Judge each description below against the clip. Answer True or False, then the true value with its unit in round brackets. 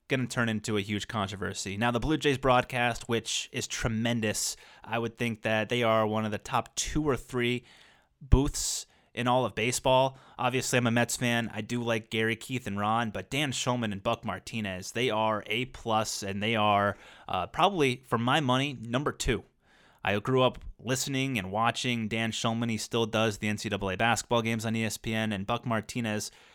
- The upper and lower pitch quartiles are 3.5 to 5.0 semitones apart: False (2.6 semitones)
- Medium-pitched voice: False (115 Hz)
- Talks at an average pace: True (190 wpm)